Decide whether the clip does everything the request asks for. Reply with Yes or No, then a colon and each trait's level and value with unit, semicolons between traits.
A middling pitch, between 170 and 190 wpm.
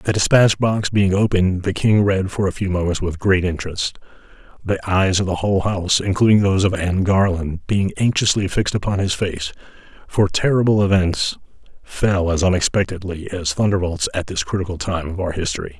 No: very low, 95 Hz; average, 180 wpm